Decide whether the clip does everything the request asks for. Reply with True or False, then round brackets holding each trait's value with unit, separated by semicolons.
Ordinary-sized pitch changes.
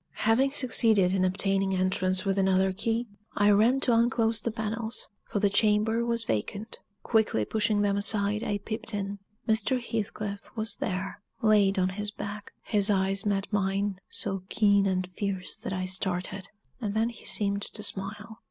False (2.3 semitones)